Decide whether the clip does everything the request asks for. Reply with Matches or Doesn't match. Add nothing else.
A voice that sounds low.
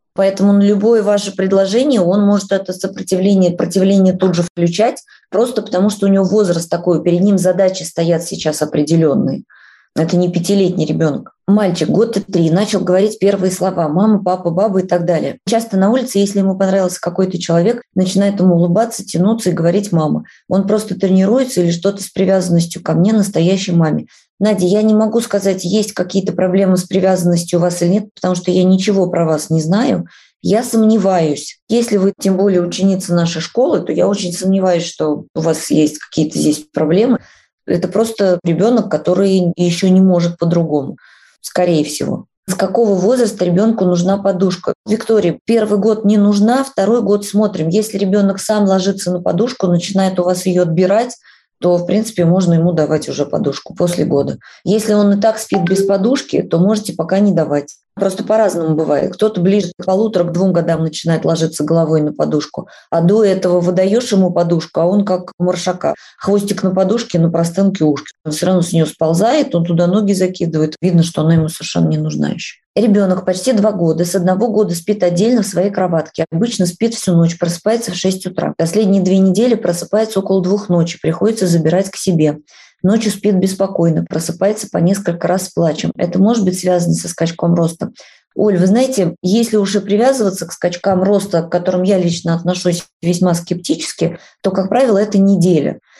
Doesn't match